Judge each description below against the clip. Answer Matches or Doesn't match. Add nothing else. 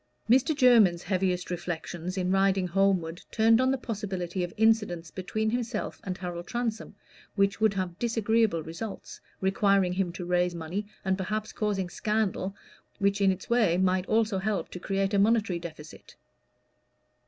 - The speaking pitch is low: Doesn't match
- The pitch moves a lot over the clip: Doesn't match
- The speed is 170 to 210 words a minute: Doesn't match